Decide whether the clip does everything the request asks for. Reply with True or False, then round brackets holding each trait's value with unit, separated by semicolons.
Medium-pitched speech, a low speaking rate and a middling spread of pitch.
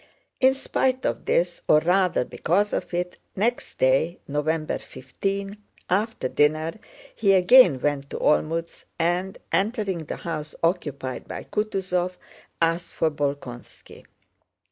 True (170 Hz; 120 wpm; 4.5 semitones)